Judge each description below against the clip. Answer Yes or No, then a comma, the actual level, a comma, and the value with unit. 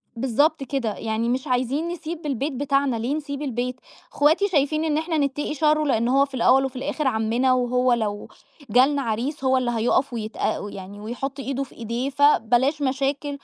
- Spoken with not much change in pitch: No, average, 3.2 semitones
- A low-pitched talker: No, very high, 265 Hz